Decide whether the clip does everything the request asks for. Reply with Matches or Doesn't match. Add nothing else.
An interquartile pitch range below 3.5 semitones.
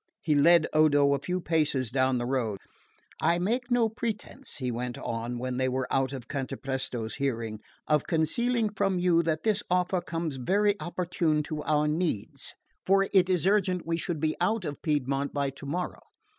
Doesn't match